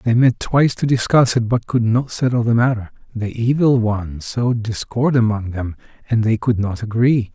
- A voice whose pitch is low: Yes, low, 115 Hz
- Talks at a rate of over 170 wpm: Yes, average, 195 wpm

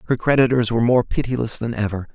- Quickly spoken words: No, average, 195 wpm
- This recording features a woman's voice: No, male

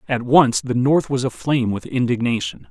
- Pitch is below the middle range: Yes, low, 125 Hz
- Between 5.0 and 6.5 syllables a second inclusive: Yes, 5.1 syllables/s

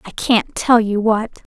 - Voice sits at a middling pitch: No, high, 220 Hz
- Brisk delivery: No, average, 190 wpm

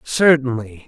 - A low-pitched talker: Yes, low, 130 Hz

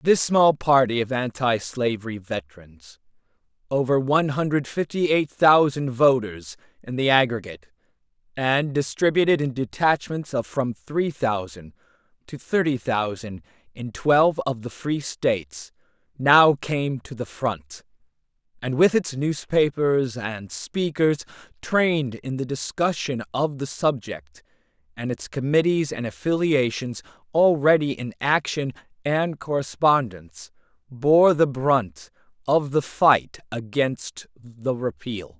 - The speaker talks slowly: Yes, slow, 120 wpm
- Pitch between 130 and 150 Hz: Yes, low, 135 Hz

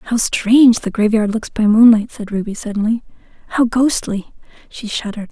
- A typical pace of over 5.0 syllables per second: Yes, 5.3 syllables/s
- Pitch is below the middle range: No, high, 220 Hz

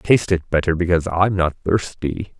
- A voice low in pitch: Yes, very low, 90 Hz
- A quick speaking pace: No, average, 175 wpm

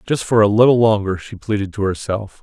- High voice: No, low, 105 Hz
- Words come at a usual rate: No, fast, 225 wpm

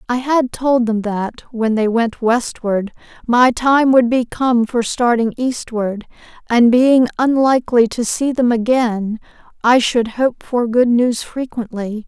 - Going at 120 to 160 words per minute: Yes, average, 155 wpm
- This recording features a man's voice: No, female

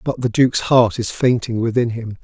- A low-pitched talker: Yes, low, 115 Hz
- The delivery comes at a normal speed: No, fast, 215 wpm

